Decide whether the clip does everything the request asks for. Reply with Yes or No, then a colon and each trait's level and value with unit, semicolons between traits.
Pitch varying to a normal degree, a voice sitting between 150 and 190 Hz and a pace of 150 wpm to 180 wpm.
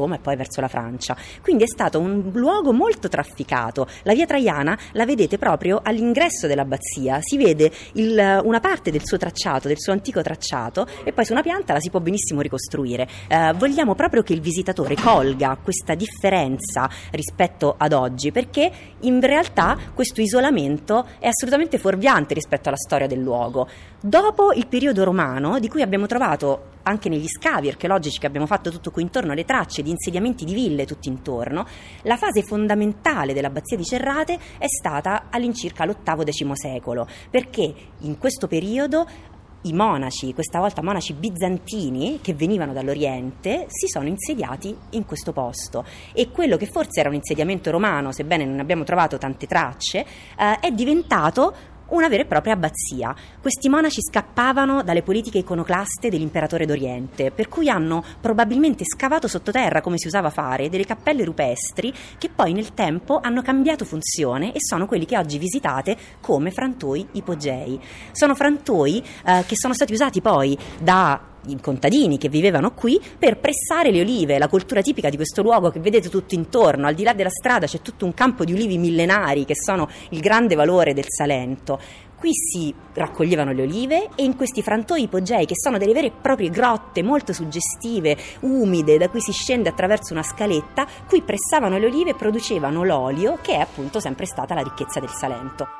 No: wide, 8.2 semitones; medium, 185 Hz; fast, 170 wpm